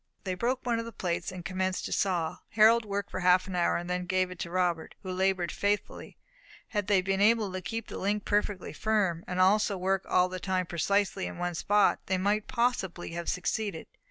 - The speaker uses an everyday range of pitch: No, narrow, 2.3 semitones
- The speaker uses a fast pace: Yes, fast, 215 wpm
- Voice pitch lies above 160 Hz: Yes, high, 190 Hz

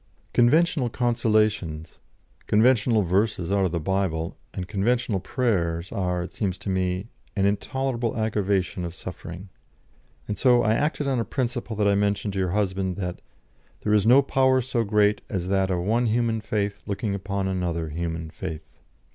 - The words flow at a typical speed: Yes, average, 165 wpm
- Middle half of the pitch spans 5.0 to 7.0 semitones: No, average, 4.0 semitones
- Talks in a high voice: No, low, 100 Hz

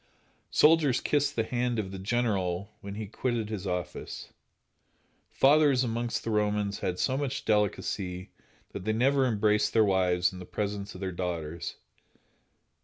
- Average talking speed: Yes, average, 150 wpm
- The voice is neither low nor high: No, low, 105 Hz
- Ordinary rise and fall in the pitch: Yes, average, 4.3 semitones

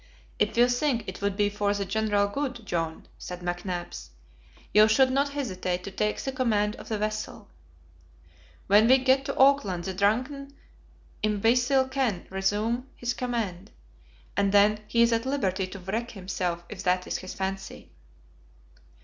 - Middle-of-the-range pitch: No, high, 210 Hz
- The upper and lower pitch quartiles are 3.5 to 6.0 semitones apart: Yes, average, 4.4 semitones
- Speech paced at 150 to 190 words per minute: Yes, average, 160 wpm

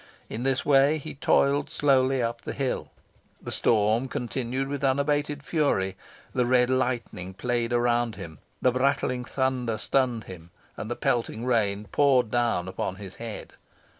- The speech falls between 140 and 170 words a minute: Yes, average, 150 wpm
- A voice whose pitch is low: Yes, low, 125 Hz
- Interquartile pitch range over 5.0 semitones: No, average, 3.1 semitones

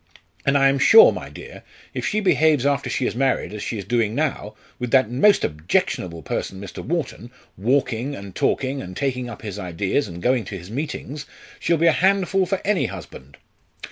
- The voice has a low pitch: Yes, low, 125 Hz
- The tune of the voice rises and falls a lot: Yes, wide, 6.6 semitones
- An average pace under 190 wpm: No, average, 195 wpm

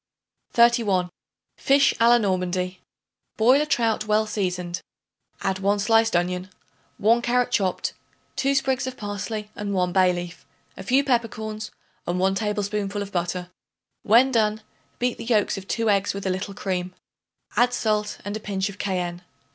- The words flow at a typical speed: Yes, average, 160 wpm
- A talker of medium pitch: No, high, 205 Hz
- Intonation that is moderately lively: Yes, average, 3.5 semitones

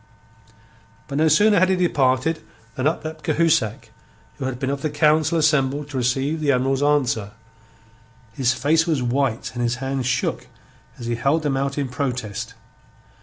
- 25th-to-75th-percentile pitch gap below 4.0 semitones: Yes, average, 3.5 semitones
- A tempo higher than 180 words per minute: No, average, 170 wpm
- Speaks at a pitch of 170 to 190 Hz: No, medium, 140 Hz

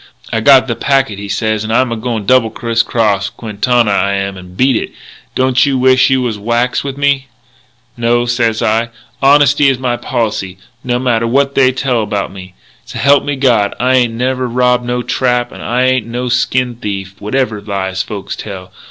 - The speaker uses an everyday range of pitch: Yes, average, 3.3 semitones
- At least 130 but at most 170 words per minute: No, average, 195 wpm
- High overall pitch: No, low, 120 Hz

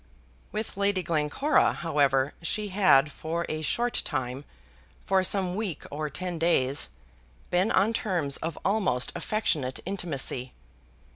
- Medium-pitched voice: Yes, medium, 170 Hz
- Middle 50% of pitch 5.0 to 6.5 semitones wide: Yes, wide, 5.5 semitones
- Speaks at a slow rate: Yes, slow, 125 wpm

